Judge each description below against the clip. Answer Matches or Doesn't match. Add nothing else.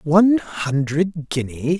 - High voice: Doesn't match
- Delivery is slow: Matches